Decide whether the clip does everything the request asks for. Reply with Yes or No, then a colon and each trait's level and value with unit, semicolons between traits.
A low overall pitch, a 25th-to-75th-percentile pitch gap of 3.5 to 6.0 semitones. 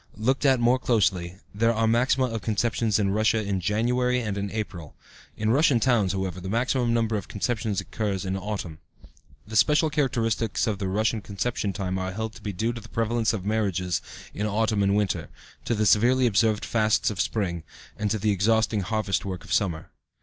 No: low, 110 Hz; average, 2.8 semitones